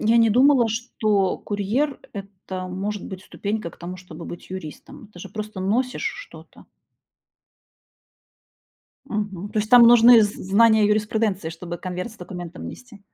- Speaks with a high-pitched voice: Yes, high, 205 Hz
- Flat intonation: No, average, 3.4 semitones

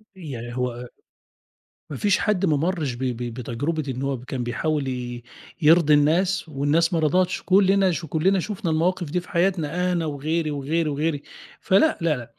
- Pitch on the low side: No, medium, 155 Hz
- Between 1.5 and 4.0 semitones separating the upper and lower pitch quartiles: No, average, 4.7 semitones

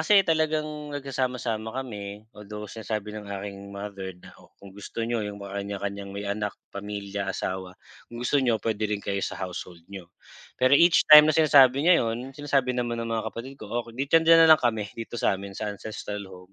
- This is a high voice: No, low, 110 Hz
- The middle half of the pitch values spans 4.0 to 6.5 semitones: Yes, average, 4.5 semitones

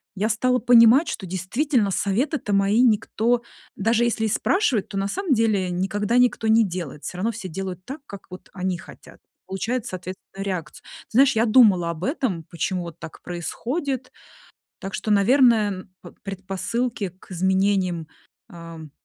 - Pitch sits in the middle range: No, high, 200 Hz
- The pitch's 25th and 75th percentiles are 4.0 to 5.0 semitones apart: Yes, average, 4.3 semitones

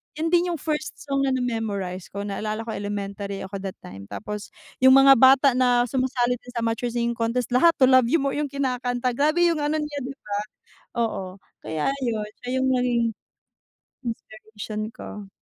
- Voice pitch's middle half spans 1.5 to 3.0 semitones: No, average, 4.1 semitones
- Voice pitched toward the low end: No, high, 245 Hz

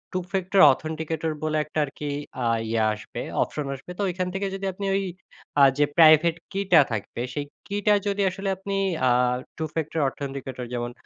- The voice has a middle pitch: Yes, medium, 160 Hz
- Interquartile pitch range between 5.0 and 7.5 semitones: Yes, wide, 5.4 semitones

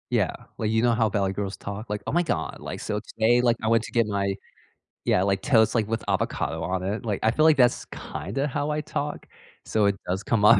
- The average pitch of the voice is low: Yes, low, 110 Hz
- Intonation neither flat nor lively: Yes, average, 3.3 semitones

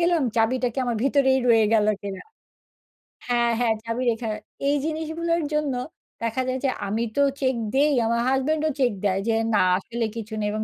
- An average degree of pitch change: Yes, average, 4.0 semitones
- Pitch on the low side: No, high, 245 Hz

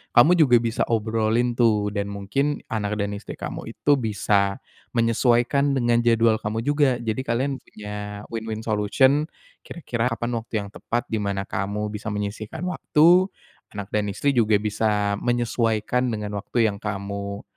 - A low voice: Yes, low, 110 Hz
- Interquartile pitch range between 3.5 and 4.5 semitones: No, average, 2.8 semitones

